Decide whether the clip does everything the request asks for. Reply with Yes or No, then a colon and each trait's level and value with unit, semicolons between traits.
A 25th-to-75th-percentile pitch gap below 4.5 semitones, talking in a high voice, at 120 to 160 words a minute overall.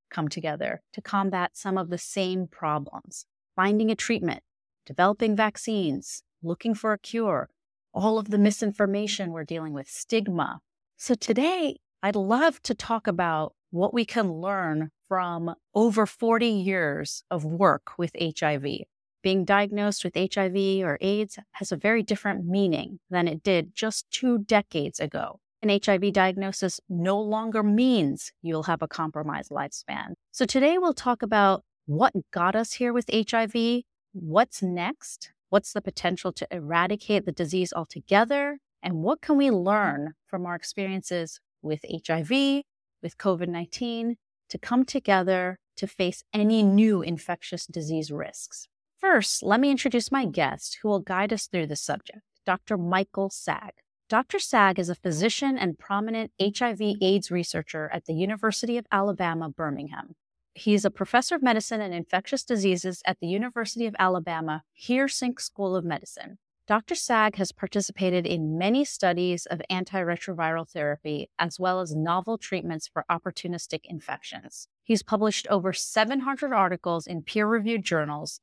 Yes: average, 4.1 semitones; high, 195 Hz; average, 145 wpm